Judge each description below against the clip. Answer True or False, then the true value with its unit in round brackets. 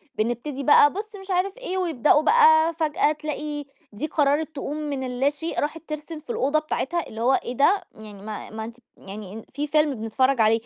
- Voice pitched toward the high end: True (295 Hz)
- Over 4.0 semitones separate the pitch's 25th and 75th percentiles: True (4.5 semitones)